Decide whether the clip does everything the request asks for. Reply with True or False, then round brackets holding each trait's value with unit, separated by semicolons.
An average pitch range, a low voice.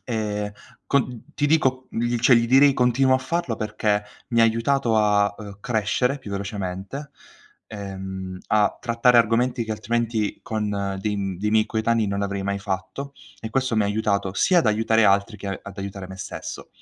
True (3.3 semitones; 110 Hz)